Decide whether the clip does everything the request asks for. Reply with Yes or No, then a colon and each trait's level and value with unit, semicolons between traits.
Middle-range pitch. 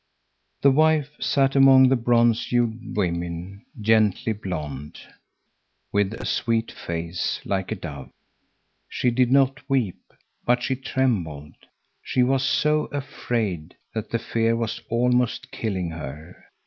No: low, 115 Hz